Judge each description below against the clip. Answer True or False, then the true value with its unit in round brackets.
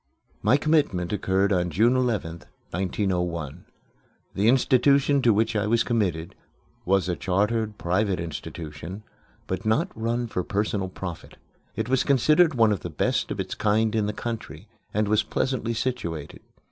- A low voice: True (105 Hz)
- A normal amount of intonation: True (4.5 semitones)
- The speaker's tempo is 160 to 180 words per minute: False (150 wpm)